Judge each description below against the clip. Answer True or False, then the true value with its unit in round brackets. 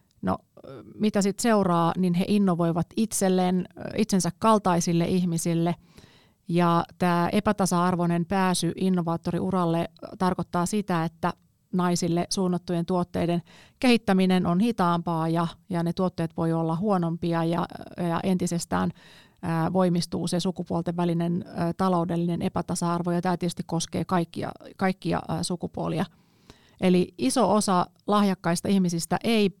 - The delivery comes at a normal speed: True (115 wpm)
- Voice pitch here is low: False (175 Hz)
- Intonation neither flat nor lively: False (1.8 semitones)